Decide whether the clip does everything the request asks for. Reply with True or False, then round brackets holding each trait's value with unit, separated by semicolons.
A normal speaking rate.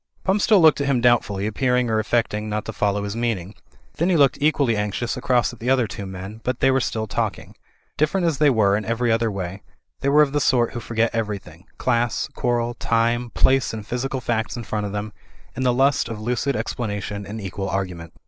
False (215 wpm)